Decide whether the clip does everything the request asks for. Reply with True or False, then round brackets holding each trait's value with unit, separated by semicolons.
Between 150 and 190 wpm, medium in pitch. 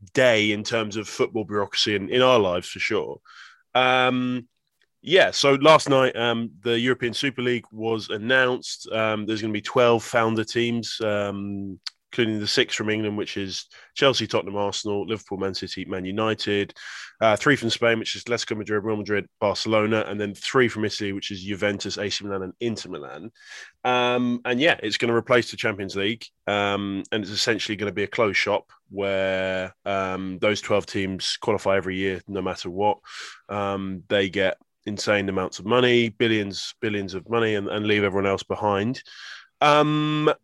False (180 wpm; 105 Hz)